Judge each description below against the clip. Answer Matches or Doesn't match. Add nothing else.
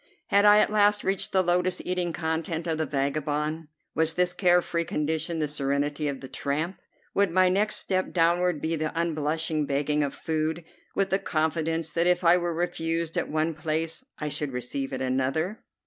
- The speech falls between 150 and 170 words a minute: Doesn't match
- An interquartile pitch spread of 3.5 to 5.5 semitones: Doesn't match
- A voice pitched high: Doesn't match